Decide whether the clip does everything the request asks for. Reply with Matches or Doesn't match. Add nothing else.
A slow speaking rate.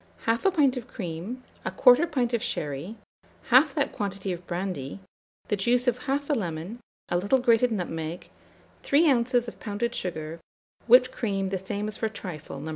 Doesn't match